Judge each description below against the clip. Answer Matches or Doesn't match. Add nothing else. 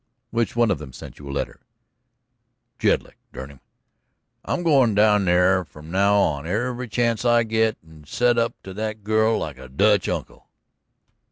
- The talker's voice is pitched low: Matches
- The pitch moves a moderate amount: Doesn't match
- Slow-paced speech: Doesn't match